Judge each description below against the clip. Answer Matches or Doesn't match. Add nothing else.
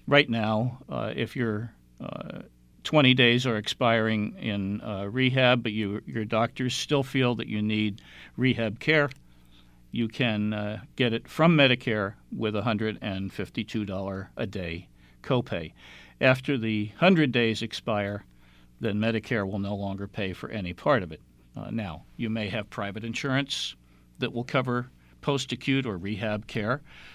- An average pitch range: Matches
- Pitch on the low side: Matches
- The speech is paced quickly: Doesn't match